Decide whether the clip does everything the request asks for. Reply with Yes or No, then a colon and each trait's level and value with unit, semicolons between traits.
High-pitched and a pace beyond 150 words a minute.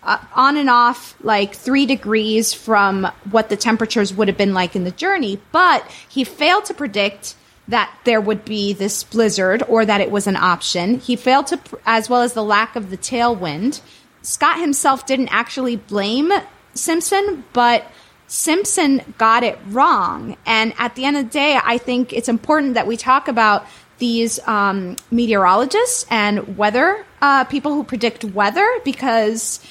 Yes: high, 235 Hz; average, 170 wpm